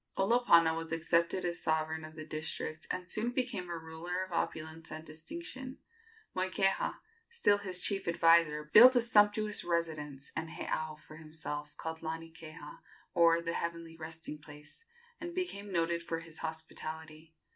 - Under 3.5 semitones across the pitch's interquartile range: Yes, average, 2.9 semitones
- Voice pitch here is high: No, medium, 165 Hz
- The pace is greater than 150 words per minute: No, average, 145 wpm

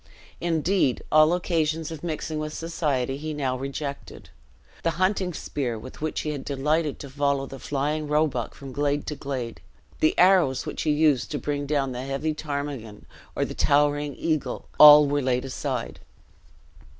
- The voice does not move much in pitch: Yes, narrow, 2.3 semitones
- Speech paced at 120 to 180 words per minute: Yes, average, 165 wpm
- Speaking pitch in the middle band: Yes, medium, 145 Hz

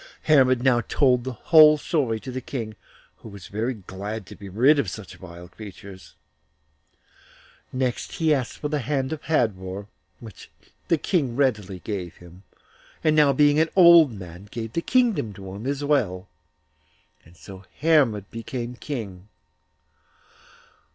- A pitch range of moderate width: No, wide, 6.6 semitones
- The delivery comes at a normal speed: Yes, average, 150 wpm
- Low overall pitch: Yes, low, 120 Hz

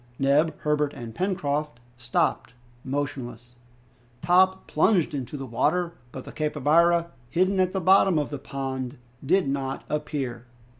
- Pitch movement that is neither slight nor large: Yes, average, 4.4 semitones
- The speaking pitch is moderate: Yes, medium, 150 Hz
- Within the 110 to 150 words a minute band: Yes, slow, 135 wpm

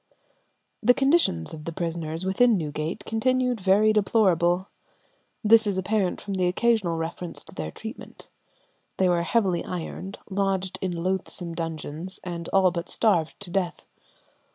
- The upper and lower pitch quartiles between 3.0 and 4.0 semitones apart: Yes, average, 3.7 semitones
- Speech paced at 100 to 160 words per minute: Yes, average, 140 wpm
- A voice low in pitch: No, medium, 185 Hz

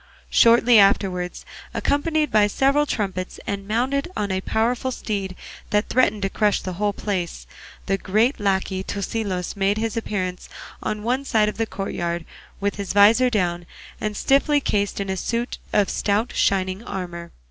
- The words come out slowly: No, average, 160 wpm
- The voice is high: Yes, high, 205 Hz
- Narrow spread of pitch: No, average, 3.3 semitones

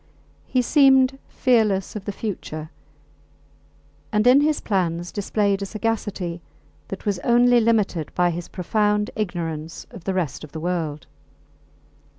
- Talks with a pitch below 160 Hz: No, high, 200 Hz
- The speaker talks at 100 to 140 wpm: Yes, slow, 135 wpm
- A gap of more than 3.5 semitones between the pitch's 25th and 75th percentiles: Yes, average, 4.6 semitones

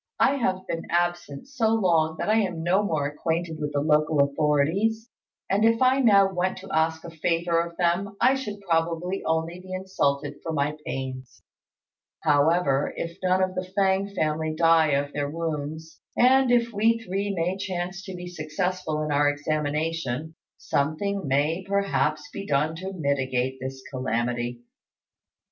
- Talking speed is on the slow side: No, average, 160 wpm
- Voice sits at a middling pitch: Yes, medium, 165 Hz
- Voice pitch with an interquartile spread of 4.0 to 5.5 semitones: Yes, average, 4.3 semitones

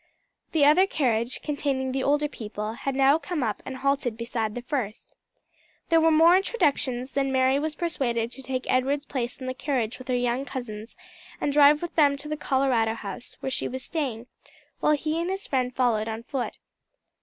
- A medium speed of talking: Yes, average, 190 wpm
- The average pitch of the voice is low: No, very high, 265 Hz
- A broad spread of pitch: No, average, 3.3 semitones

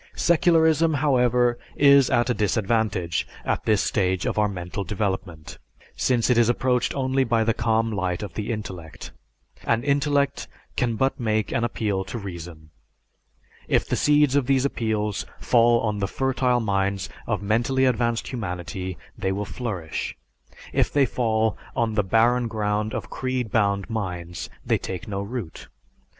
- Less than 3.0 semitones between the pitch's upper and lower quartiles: No, average, 4.0 semitones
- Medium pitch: No, low, 110 Hz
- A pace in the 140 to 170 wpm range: Yes, average, 155 wpm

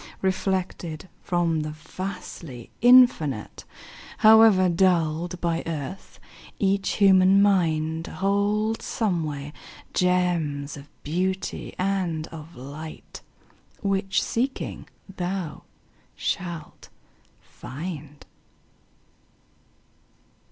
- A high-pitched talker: No, medium, 180 Hz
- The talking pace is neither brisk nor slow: No, slow, 75 wpm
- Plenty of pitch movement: No, average, 3.7 semitones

